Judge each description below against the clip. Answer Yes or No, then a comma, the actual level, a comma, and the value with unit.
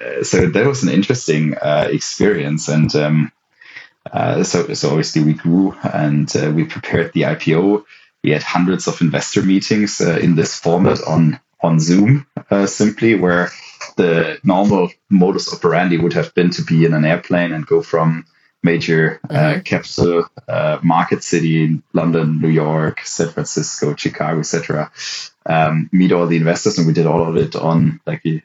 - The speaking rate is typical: Yes, average, 165 wpm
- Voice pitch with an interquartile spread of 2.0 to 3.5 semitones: Yes, average, 2.9 semitones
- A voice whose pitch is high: No, very low, 85 Hz